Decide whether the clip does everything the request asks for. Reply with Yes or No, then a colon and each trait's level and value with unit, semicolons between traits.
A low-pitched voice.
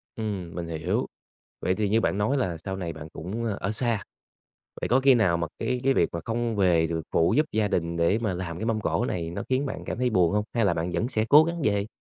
Yes: low, 100 Hz